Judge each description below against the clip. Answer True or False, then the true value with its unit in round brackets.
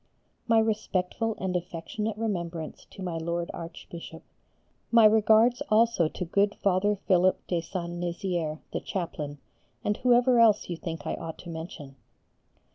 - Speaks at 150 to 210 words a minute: False (140 wpm)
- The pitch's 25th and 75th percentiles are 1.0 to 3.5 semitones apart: False (4.2 semitones)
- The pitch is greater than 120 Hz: True (185 Hz)